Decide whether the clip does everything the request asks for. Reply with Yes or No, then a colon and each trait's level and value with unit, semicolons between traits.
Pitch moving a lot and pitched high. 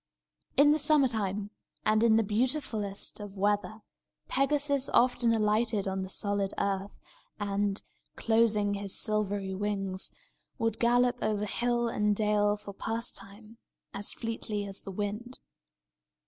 No: narrow, 2.5 semitones; high, 210 Hz